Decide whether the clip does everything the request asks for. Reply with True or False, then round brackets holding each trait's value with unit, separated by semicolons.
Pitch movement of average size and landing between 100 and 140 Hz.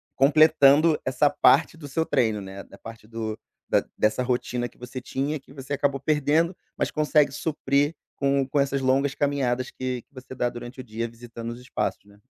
True (3.0 semitones; 135 Hz)